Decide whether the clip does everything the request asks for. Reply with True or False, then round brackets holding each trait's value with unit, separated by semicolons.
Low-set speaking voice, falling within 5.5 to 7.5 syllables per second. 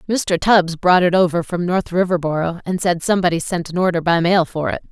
False (175 Hz; 5.6 syllables/s)